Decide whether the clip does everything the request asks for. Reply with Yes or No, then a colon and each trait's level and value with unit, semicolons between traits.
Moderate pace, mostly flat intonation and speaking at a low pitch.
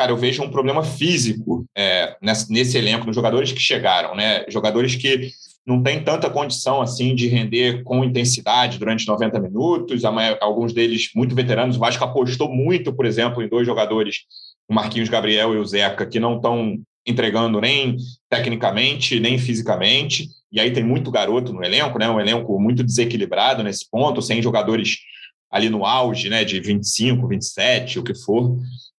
Yes: average, 170 wpm; narrow, 2.2 semitones; low, 120 Hz